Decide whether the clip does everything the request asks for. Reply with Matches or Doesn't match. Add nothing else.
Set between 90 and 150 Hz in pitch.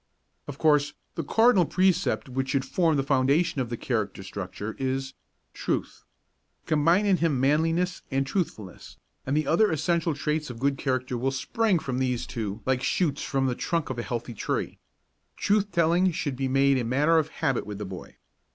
Matches